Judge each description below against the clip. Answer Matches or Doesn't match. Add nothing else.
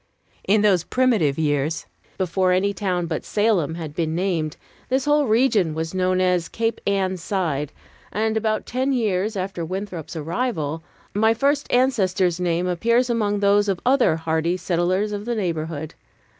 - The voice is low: Doesn't match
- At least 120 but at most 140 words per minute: Doesn't match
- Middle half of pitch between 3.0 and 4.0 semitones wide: Doesn't match